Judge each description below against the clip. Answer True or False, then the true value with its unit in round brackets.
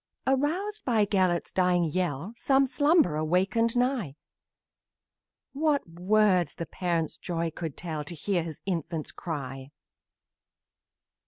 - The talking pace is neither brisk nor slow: False (110 wpm)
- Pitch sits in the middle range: True (180 Hz)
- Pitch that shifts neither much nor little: False (6.2 semitones)